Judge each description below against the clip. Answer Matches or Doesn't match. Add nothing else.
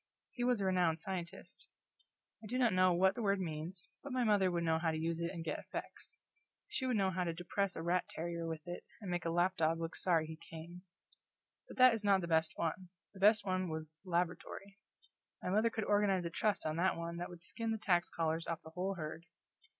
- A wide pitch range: Doesn't match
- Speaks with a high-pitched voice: Doesn't match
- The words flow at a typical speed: Doesn't match